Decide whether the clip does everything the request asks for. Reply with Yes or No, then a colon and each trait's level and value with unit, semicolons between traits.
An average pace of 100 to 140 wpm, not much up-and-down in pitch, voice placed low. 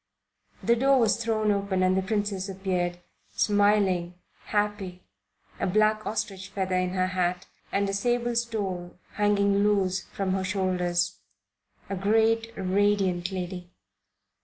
No: slow, 135 wpm; narrow, 2.2 semitones; high, 195 Hz